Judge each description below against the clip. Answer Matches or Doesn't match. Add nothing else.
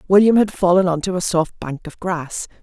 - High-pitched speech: Doesn't match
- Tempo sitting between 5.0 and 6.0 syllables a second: Matches